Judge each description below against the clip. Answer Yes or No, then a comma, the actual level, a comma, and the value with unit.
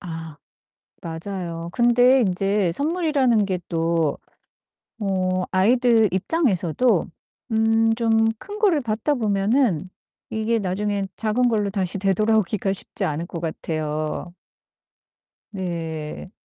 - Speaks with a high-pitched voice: Yes, high, 200 Hz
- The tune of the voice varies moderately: Yes, average, 4.9 semitones